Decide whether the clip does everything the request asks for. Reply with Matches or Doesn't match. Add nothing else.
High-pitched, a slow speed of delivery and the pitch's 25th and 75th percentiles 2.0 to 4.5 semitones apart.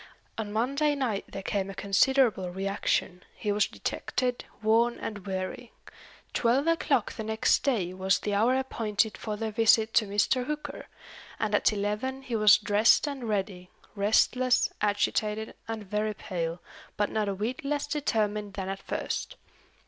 Doesn't match